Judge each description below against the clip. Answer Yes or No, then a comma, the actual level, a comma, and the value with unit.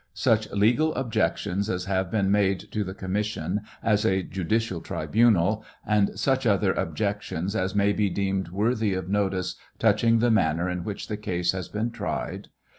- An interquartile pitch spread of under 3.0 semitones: Yes, narrow, 2.6 semitones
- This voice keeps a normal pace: Yes, average, 165 wpm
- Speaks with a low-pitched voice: Yes, low, 100 Hz